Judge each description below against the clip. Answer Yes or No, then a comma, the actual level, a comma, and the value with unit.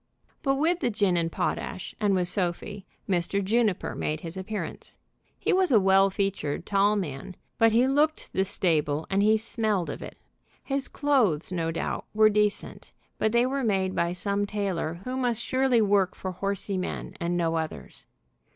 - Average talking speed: Yes, average, 175 wpm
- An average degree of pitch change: Yes, average, 4.1 semitones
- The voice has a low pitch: No, high, 200 Hz